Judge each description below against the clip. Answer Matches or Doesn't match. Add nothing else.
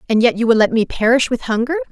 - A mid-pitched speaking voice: Doesn't match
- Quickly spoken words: Matches